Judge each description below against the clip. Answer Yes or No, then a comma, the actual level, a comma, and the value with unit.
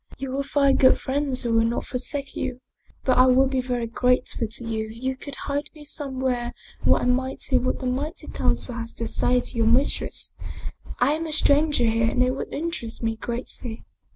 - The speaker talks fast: Yes, fast, 210 wpm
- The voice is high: Yes, very high, 255 Hz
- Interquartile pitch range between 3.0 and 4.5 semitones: No, narrow, 2.6 semitones